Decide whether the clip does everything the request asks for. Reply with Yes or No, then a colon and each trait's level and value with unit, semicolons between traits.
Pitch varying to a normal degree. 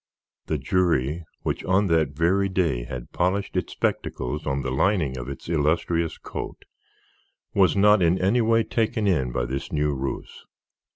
No: wide, 6.0 semitones